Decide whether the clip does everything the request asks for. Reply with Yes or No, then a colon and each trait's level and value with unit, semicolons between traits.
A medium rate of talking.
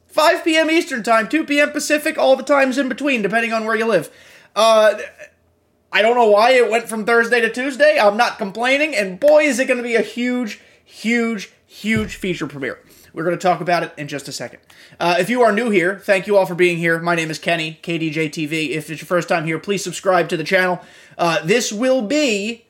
No: fast, 225 wpm